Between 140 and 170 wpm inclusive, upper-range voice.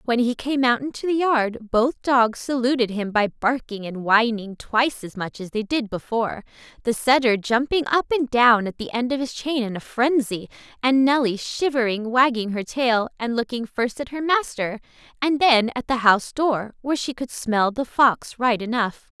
No: average, 195 wpm; high, 240 Hz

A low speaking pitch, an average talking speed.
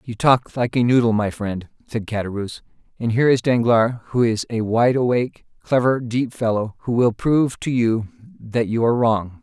Yes: low, 120 Hz; average, 190 wpm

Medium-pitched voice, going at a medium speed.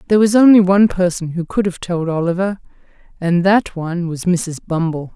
Yes: medium, 180 Hz; average, 185 wpm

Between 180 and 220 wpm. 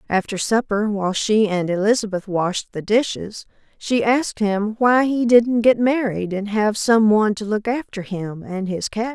Yes: average, 185 wpm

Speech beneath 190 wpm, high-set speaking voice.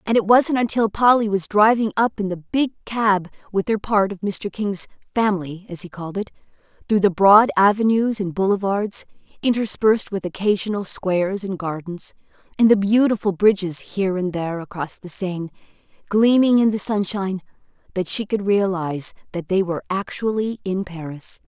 Yes: average, 165 wpm; high, 200 Hz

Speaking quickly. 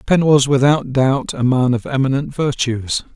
No: average, 170 wpm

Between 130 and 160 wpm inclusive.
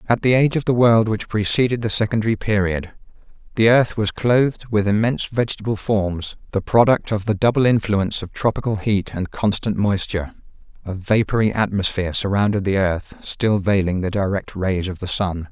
No: average, 175 wpm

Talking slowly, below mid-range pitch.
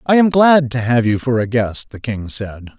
No: fast, 260 wpm; low, 125 Hz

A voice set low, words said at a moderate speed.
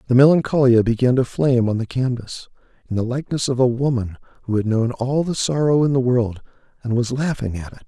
No: low, 125 Hz; fast, 215 wpm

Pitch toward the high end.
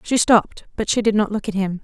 Yes: high, 205 Hz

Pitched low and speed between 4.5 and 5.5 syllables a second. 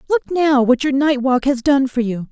No: very high, 265 Hz; 4.7 syllables/s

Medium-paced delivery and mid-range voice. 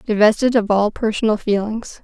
No: average, 145 wpm; high, 215 Hz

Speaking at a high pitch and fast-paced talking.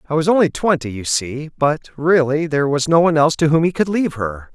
No: medium, 150 Hz; fast, 250 wpm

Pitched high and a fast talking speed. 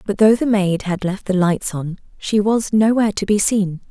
Yes: high, 200 Hz; fast, 230 wpm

